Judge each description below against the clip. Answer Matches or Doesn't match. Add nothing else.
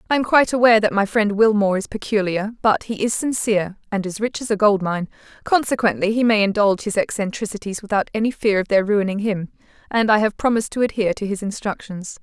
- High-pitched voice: Matches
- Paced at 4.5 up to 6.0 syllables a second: Doesn't match